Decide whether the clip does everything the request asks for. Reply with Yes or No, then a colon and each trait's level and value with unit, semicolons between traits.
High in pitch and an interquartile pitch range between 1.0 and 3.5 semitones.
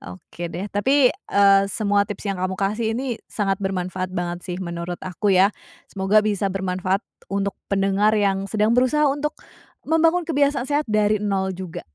Yes: high, 200 Hz; average, 3.0 semitones